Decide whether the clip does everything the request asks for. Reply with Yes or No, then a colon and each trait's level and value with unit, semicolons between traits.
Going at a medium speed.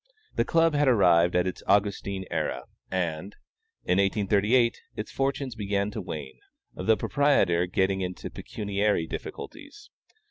No: slow, 130 wpm